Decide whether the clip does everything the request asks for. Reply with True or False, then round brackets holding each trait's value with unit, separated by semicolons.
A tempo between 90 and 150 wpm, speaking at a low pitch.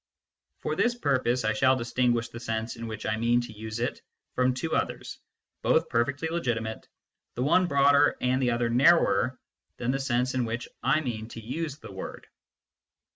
False (180 wpm; 125 Hz)